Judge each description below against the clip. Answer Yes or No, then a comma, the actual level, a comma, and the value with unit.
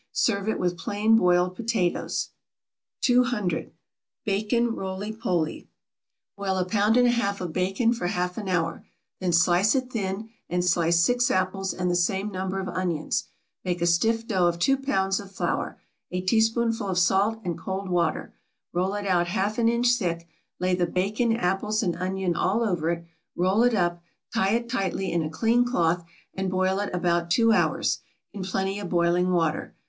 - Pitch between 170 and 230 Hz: Yes, high, 190 Hz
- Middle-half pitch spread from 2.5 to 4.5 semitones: Yes, average, 3.7 semitones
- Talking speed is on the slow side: No, average, 180 wpm